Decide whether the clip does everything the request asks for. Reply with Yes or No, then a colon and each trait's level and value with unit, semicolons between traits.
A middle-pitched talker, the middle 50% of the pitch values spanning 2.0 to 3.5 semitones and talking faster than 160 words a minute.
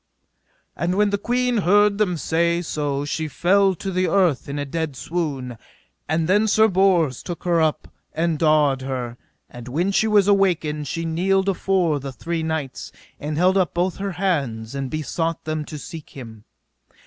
No: medium, 165 Hz; average, 4.7 semitones; average, 175 wpm